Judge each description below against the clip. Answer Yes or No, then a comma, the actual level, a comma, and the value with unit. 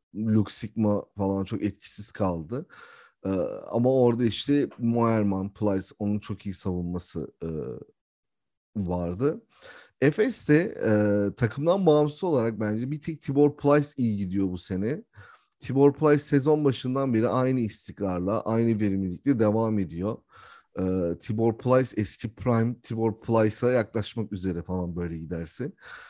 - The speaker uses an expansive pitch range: No, average, 4.8 semitones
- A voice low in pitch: Yes, low, 110 Hz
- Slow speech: No, average, 125 wpm